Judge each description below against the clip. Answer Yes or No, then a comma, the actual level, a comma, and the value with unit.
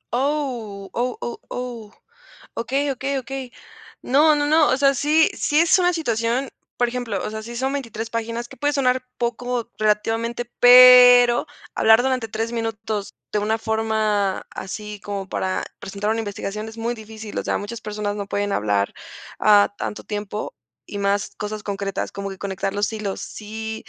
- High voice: Yes, high, 225 Hz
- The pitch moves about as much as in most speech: Yes, average, 3.2 semitones